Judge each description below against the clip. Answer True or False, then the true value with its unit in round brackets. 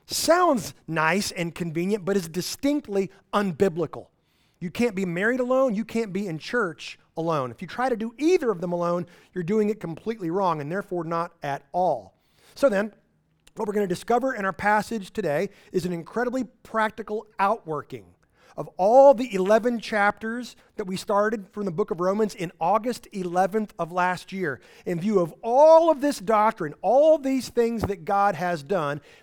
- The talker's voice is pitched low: False (200 Hz)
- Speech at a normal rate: True (180 wpm)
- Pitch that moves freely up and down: False (4.2 semitones)